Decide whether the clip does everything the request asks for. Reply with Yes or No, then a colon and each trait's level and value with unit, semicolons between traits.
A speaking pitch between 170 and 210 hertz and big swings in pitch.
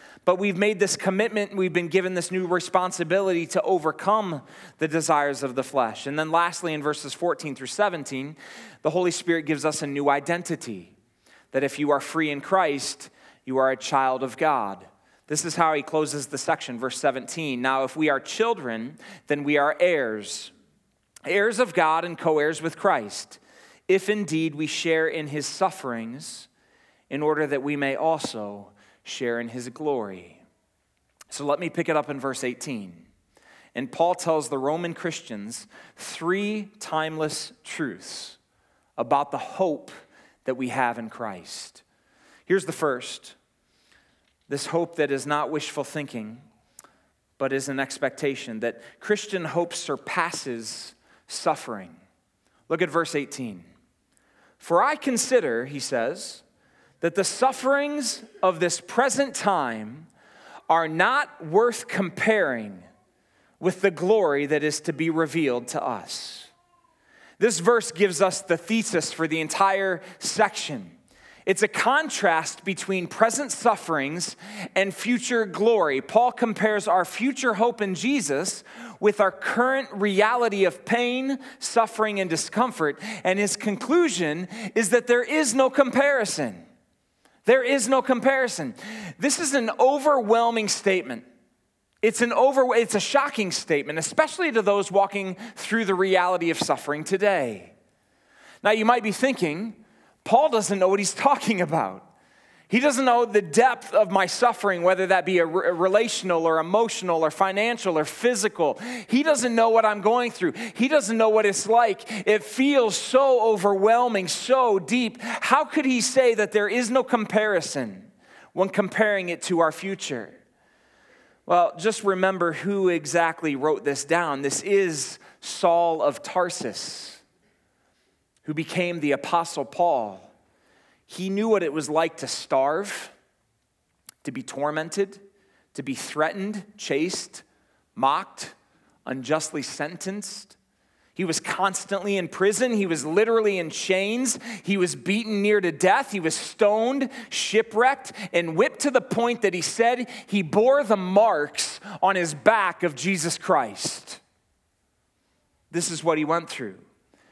Yes: medium, 185 Hz; wide, 6.1 semitones